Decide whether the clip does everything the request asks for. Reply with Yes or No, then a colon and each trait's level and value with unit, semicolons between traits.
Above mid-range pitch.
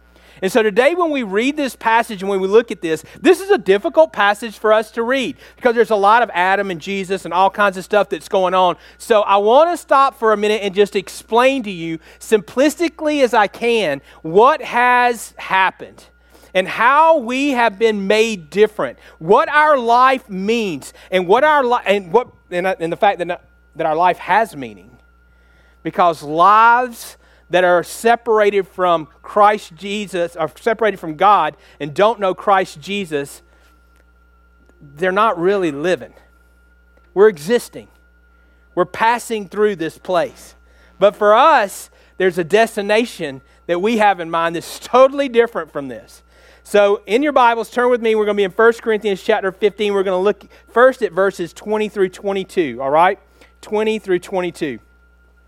Yes: high, 205 Hz